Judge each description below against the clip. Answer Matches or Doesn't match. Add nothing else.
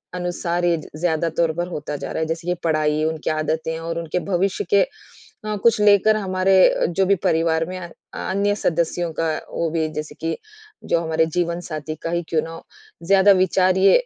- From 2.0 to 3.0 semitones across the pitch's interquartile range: Matches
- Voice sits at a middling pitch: Matches